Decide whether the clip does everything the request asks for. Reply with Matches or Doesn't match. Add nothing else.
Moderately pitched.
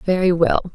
Matches